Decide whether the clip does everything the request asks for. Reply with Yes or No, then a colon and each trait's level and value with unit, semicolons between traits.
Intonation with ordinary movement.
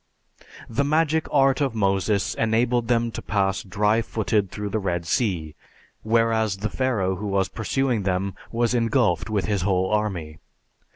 Yes: average, 3.3 semitones